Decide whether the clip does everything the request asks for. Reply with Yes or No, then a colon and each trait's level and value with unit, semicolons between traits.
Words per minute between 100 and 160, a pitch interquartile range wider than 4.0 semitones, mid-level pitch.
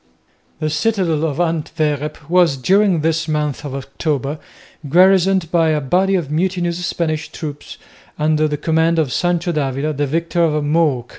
No: average, 150 wpm; narrow, 2.6 semitones; medium, 160 Hz